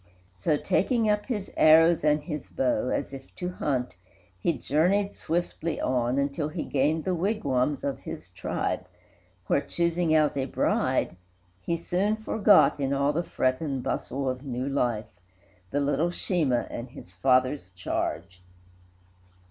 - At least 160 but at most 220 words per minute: No, average, 150 wpm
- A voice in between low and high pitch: Yes, medium, 145 Hz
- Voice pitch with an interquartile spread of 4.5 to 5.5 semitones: Yes, average, 4.8 semitones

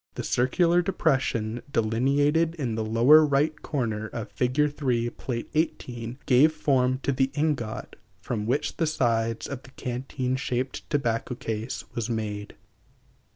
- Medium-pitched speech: No, low, 125 Hz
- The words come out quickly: No, average, 150 wpm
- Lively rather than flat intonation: No, average, 4.0 semitones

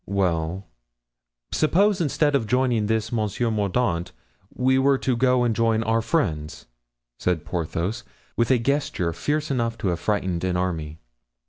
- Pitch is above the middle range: No, low, 115 Hz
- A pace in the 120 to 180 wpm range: Yes, average, 145 wpm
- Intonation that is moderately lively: No, wide, 6.3 semitones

